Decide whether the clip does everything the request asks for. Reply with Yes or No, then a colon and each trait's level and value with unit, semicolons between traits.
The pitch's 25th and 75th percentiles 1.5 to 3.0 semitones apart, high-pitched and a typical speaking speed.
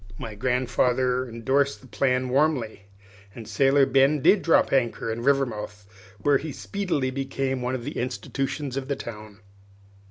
No: average, 2.7 semitones; low, 130 Hz; average, 150 wpm